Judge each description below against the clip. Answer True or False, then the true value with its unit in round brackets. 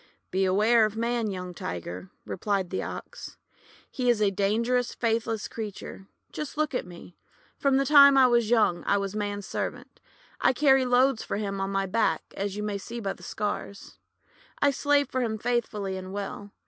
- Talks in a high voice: True (215 Hz)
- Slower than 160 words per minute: False (180 wpm)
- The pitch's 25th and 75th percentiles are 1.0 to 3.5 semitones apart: False (3.9 semitones)